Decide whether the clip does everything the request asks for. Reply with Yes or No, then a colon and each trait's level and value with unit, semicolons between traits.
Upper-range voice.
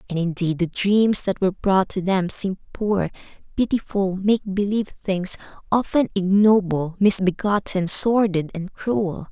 Yes: high, 195 Hz